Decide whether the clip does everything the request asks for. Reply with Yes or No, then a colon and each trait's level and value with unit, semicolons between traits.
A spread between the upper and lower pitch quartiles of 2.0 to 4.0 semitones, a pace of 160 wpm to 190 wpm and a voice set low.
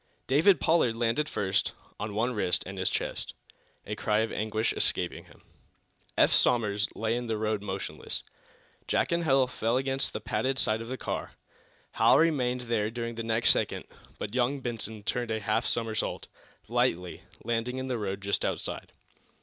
Yes: average, 2.9 semitones; average, 170 wpm; low, 115 Hz